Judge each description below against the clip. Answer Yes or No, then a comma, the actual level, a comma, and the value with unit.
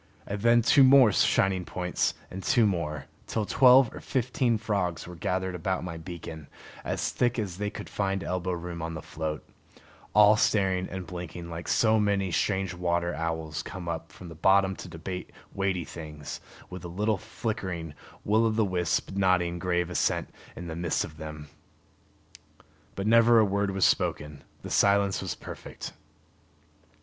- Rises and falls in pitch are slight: No, average, 3.3 semitones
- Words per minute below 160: No, average, 165 wpm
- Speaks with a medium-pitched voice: No, very low, 95 Hz